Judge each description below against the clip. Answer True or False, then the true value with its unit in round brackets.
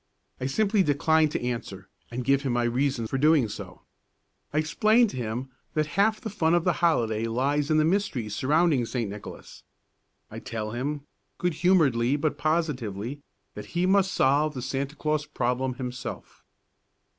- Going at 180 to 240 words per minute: False (165 wpm)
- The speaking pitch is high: False (145 Hz)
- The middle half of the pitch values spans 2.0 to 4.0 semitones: False (4.6 semitones)